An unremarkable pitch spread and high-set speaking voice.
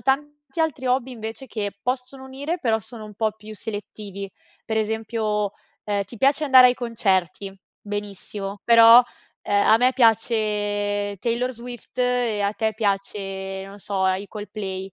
Yes: average, 3.4 semitones; high, 220 Hz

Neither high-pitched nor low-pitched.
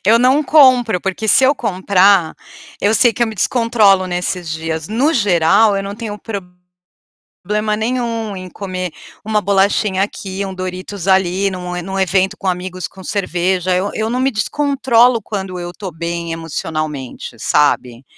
No: high, 195 Hz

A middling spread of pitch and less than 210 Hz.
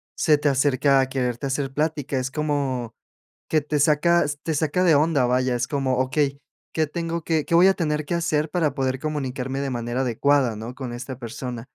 Yes: average, 3.0 semitones; medium, 140 Hz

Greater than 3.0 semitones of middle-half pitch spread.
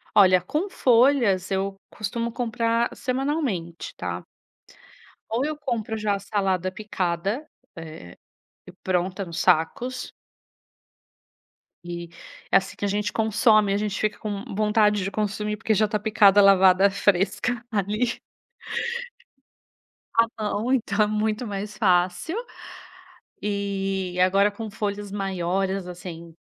No: average, 2.7 semitones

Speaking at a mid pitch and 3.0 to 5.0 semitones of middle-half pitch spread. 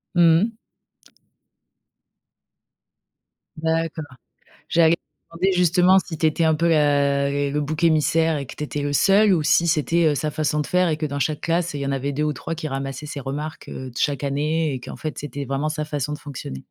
No: medium, 150 Hz; narrow, 2.5 semitones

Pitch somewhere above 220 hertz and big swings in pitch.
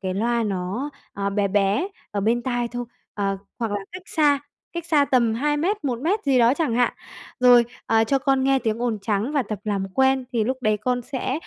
No: high, 240 Hz; average, 4.2 semitones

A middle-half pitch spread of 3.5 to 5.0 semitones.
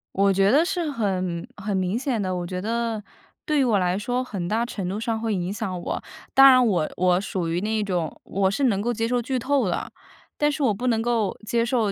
Yes: average, 4.3 semitones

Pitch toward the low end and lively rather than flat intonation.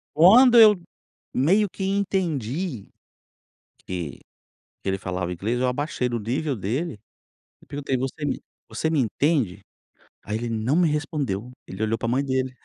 Yes: low, 130 Hz; wide, 6.3 semitones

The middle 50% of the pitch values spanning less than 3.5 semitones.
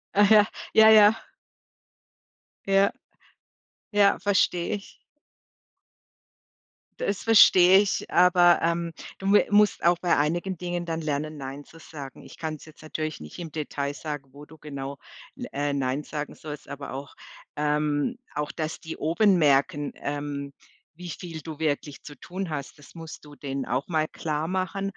No: average, 3.8 semitones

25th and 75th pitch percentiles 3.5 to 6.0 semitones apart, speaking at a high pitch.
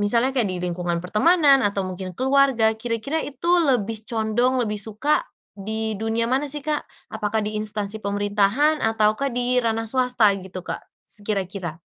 Yes: average, 4.0 semitones; high, 220 Hz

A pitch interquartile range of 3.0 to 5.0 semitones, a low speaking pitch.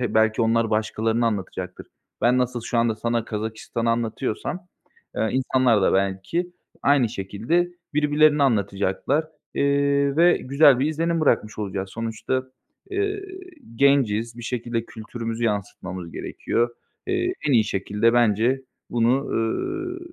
Yes: average, 4.4 semitones; low, 120 Hz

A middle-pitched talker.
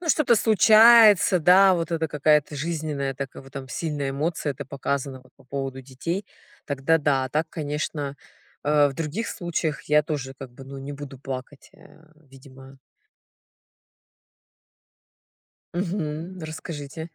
Yes: medium, 150 Hz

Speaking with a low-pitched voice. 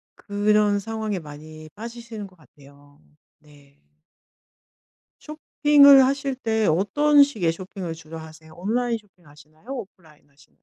No: high, 195 Hz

